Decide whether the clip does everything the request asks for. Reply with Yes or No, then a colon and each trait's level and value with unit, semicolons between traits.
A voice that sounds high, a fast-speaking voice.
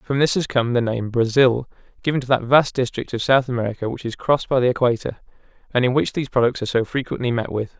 No: low, 125 Hz; fast, 240 wpm